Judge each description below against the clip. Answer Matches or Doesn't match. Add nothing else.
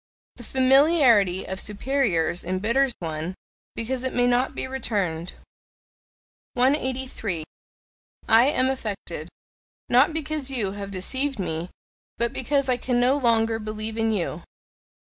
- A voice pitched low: Doesn't match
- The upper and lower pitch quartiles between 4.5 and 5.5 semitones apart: Matches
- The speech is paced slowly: Matches